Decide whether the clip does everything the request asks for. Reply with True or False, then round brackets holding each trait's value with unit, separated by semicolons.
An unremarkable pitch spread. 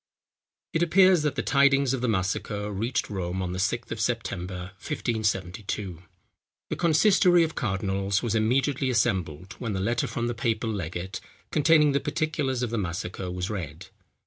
False (6.3 semitones)